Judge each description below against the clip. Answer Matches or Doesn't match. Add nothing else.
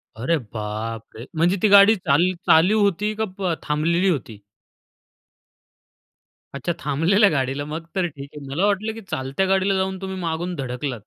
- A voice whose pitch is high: Doesn't match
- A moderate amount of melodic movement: Doesn't match